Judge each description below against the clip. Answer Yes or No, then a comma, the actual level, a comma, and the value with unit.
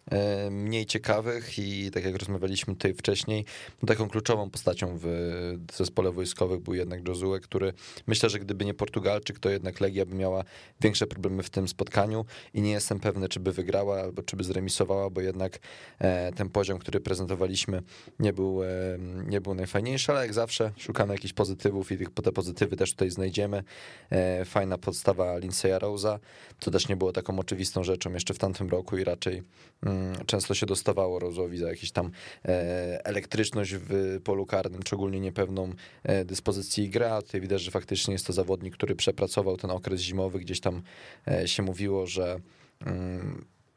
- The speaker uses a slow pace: No, fast, 160 wpm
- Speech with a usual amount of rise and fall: No, narrow, 1.8 semitones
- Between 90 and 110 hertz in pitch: Yes, very low, 95 Hz